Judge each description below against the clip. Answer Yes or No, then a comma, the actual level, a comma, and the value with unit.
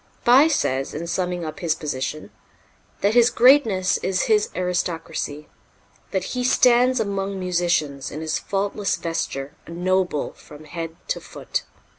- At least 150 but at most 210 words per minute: No, average, 140 wpm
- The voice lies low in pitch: No, medium, 180 Hz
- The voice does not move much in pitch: No, average, 4.9 semitones